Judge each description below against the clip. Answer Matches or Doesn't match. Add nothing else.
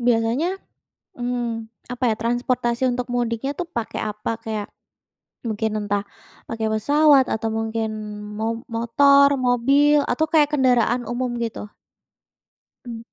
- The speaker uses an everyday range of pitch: Matches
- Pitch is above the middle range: Matches